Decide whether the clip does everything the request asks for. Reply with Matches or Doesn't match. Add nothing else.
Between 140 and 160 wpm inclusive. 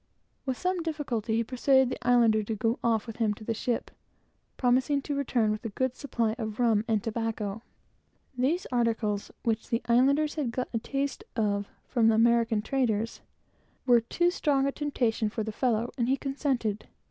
Doesn't match